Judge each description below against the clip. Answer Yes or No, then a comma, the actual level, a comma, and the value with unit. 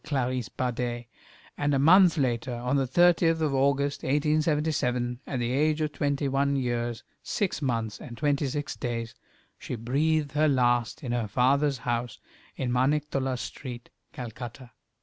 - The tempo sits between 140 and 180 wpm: Yes, average, 150 wpm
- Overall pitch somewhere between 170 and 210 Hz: No, low, 135 Hz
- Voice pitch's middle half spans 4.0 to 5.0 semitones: No, average, 3.2 semitones